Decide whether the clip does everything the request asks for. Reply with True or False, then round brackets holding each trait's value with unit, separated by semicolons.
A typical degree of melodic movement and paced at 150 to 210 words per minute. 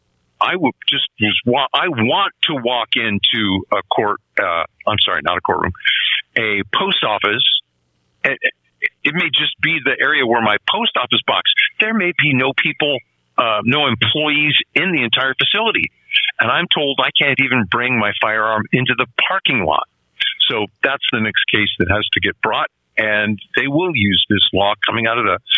False (6.4 semitones; 180 wpm)